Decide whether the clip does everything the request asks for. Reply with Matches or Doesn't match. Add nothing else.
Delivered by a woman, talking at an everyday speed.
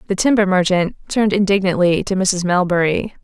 Matches